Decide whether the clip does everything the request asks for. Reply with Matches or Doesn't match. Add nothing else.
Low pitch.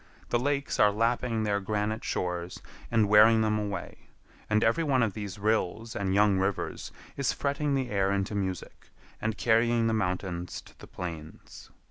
Matches